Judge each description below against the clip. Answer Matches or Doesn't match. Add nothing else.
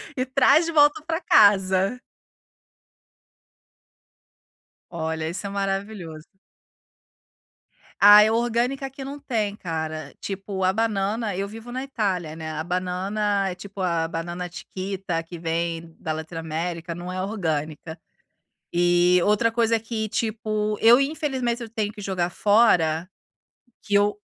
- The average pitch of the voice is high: Matches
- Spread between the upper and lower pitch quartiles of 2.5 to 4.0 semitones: Doesn't match